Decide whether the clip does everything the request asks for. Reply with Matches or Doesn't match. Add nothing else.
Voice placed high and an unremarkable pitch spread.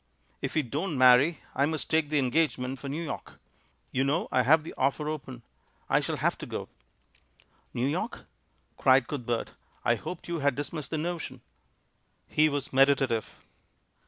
Doesn't match